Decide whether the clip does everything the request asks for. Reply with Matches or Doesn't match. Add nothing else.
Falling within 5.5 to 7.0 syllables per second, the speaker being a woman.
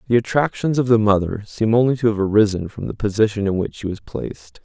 Doesn't match